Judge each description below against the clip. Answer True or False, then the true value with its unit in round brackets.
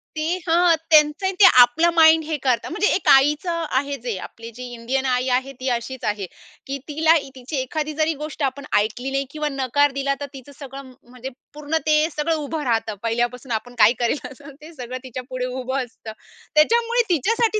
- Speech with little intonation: False (3.7 semitones)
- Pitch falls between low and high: False (275 Hz)